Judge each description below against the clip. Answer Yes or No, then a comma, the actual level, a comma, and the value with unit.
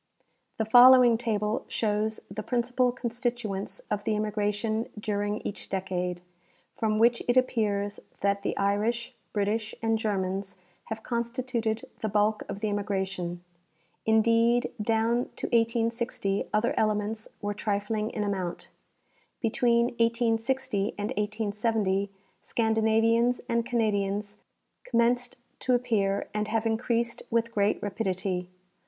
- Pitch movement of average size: No, narrow, 2.3 semitones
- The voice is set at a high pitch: Yes, high, 220 Hz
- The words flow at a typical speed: No, slow, 115 wpm